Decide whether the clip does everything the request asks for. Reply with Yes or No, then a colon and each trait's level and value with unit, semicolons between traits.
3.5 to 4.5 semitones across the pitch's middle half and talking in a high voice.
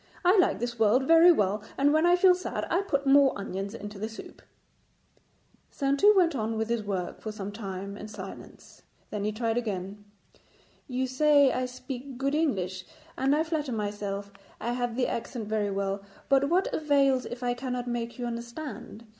No: average, 5.1 semitones; high, 245 Hz